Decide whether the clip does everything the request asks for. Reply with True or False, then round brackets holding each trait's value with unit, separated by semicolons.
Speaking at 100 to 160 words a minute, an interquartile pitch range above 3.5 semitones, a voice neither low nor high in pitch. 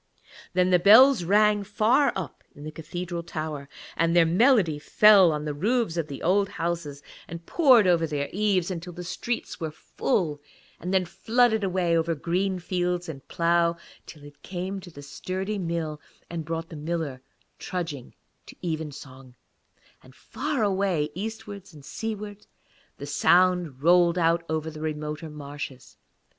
True (155 wpm; 3.9 semitones; 170 Hz)